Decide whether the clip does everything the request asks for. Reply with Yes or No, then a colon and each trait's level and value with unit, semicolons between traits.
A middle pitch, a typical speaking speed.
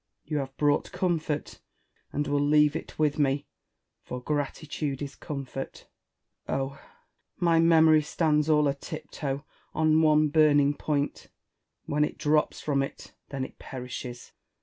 Yes: medium, 150 Hz; average, 145 wpm